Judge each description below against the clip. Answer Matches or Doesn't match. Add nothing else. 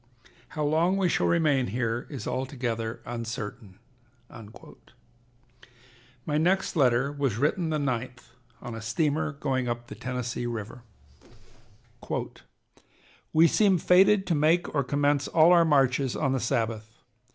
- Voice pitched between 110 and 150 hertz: Matches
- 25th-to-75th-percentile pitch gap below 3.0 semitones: Doesn't match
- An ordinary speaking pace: Doesn't match